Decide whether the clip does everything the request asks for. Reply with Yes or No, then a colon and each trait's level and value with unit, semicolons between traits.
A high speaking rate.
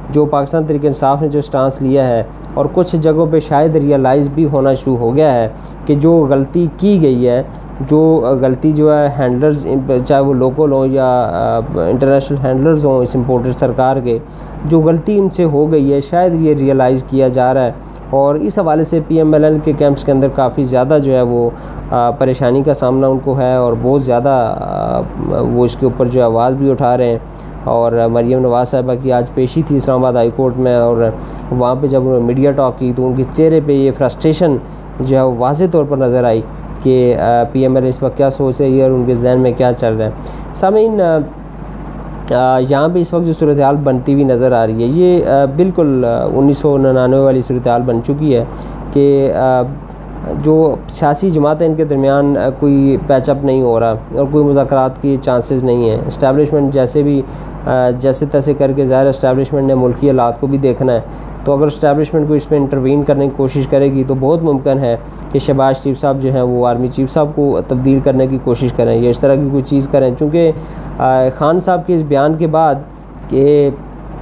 Yes: fast, 210 wpm